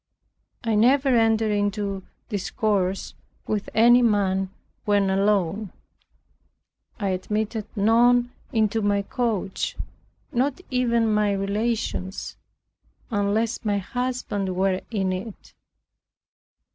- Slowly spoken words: Yes, slow, 95 wpm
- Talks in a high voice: Yes, high, 210 Hz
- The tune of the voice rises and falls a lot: No, narrow, 2.6 semitones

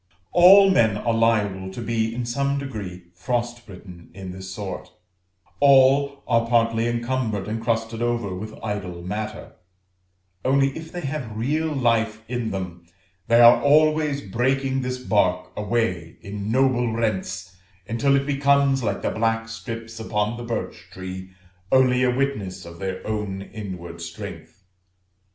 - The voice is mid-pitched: No, low, 115 Hz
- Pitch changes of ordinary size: Yes, average, 4.8 semitones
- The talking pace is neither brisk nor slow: Yes, average, 145 wpm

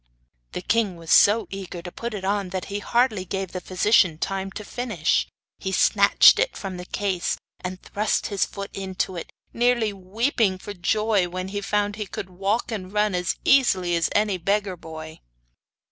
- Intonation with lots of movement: No, narrow, 2.5 semitones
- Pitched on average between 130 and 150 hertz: No, high, 195 Hz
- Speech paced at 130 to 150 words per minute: No, average, 180 wpm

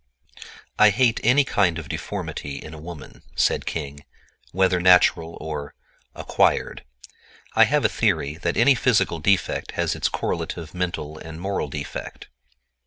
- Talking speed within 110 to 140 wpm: Yes, slow, 135 wpm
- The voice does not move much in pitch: No, average, 4.1 semitones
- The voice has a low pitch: Yes, very low, 85 Hz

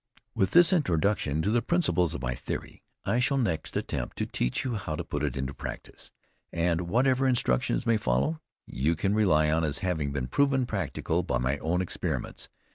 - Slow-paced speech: No, average, 190 wpm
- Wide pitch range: Yes, wide, 8.8 semitones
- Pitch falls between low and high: No, very low, 90 Hz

